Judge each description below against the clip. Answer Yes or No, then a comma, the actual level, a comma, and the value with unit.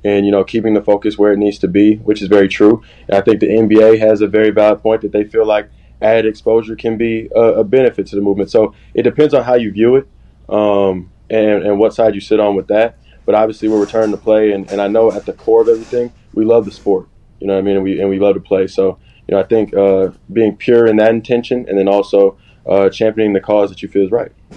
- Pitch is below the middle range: Yes, low, 105 Hz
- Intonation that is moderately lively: No, narrow, 1.9 semitones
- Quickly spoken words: Yes, fast, 270 wpm